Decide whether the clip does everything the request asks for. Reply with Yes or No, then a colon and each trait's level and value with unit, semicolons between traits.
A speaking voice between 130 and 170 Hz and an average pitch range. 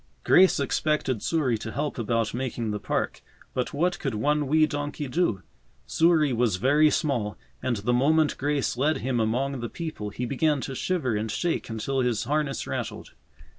Yes: low, 135 Hz; average, 4.6 semitones